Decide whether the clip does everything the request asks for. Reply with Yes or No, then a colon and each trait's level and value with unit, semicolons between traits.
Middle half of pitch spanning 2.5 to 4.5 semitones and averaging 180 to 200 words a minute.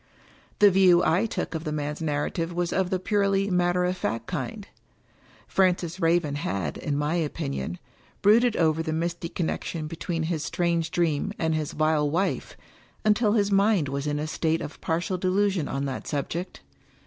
No: average, 3.5 semitones; average, 170 wpm